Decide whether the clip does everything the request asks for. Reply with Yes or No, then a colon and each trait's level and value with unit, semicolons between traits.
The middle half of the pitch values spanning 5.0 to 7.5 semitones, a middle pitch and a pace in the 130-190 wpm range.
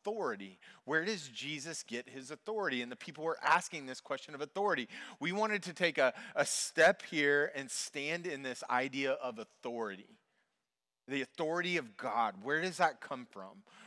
Yes: wide, 5.6 semitones; medium, 150 Hz; average, 175 wpm